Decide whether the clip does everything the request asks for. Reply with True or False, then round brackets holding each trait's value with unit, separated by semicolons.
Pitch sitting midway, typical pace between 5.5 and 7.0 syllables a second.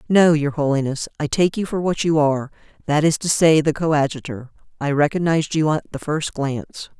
True (150 Hz; 5.6 syllables/s)